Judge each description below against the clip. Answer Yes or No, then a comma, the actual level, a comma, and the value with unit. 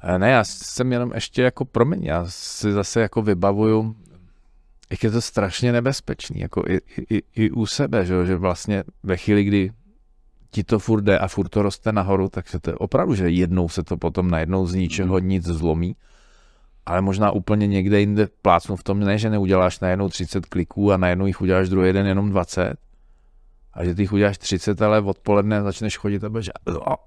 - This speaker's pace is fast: Yes, fast, 190 wpm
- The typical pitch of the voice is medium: No, low, 100 Hz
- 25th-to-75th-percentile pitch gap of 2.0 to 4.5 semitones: Yes, narrow, 2.6 semitones